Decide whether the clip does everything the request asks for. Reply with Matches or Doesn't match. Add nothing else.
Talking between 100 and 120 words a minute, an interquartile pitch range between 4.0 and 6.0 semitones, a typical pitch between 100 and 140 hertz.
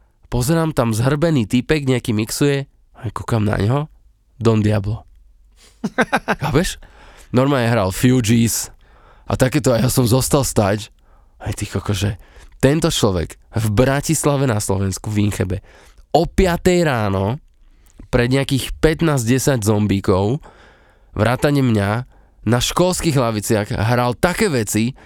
Matches